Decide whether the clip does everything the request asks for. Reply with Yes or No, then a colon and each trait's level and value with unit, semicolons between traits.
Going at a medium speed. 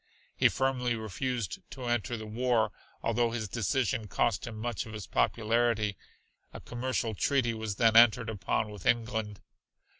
Yes: average, 150 wpm